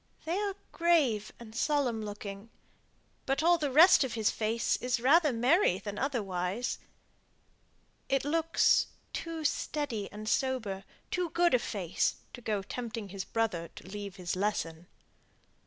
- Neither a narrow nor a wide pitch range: No, wide, 6.2 semitones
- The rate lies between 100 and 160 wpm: Yes, average, 140 wpm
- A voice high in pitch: Yes, high, 230 Hz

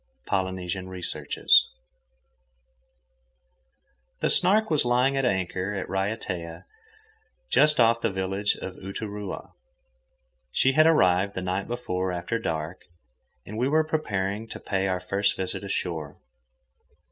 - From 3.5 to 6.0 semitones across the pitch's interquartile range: Yes, average, 4.1 semitones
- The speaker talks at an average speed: No, slow, 120 wpm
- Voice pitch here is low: Yes, very low, 95 Hz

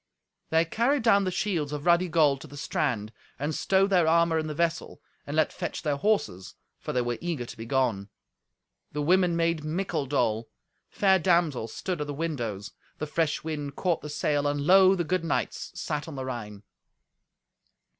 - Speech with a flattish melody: No, average, 3.7 semitones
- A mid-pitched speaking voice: Yes, medium, 155 Hz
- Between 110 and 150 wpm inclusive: No, average, 185 wpm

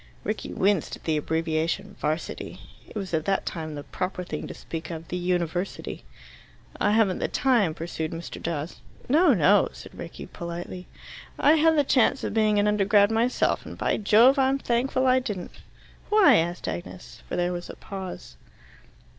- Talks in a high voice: Yes, high, 195 Hz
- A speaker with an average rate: Yes, average, 170 wpm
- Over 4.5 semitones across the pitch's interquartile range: Yes, average, 5.1 semitones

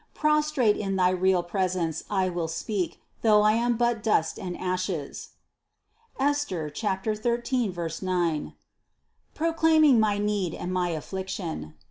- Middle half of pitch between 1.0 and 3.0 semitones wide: No, average, 4.8 semitones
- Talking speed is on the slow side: Yes, slow, 125 wpm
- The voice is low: No, high, 190 Hz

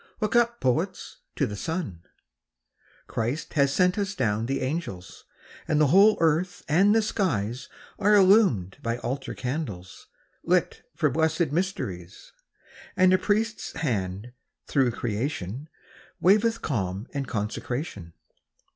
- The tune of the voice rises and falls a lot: Yes, wide, 8.9 semitones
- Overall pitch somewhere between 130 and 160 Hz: Yes, medium, 140 Hz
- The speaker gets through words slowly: Yes, slow, 130 wpm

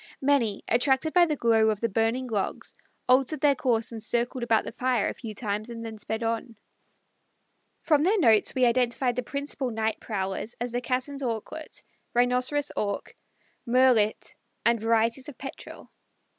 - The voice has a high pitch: Yes, high, 240 Hz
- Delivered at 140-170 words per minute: Yes, average, 160 wpm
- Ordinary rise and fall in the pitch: Yes, average, 3.0 semitones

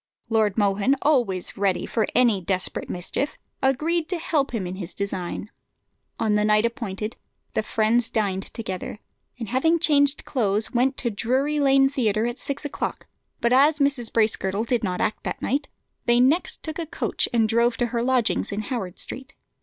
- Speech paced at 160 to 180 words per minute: Yes, average, 175 wpm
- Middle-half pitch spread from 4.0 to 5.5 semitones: Yes, average, 4.5 semitones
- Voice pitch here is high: Yes, high, 235 Hz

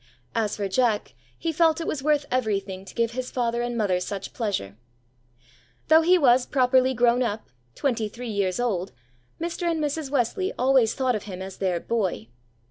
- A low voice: No, high, 240 Hz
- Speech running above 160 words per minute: Yes, average, 180 wpm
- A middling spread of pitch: Yes, average, 4.9 semitones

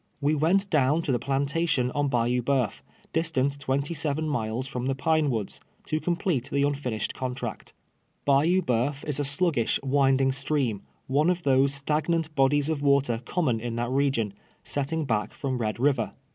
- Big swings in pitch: No, average, 3.2 semitones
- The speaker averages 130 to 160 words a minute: No, average, 170 wpm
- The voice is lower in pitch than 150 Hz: Yes, medium, 140 Hz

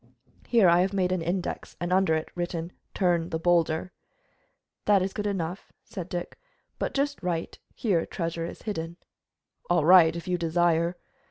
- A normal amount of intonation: No, narrow, 2.1 semitones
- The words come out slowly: No, average, 165 wpm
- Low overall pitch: No, medium, 175 Hz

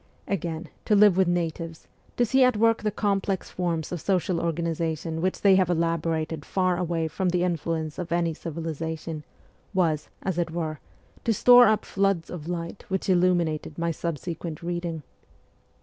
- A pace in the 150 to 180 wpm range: Yes, average, 160 wpm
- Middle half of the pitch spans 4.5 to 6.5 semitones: No, narrow, 2.4 semitones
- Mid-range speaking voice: Yes, medium, 170 Hz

